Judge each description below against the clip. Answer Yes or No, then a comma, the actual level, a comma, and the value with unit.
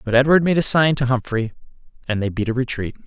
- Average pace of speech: No, fast, 235 wpm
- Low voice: Yes, low, 125 Hz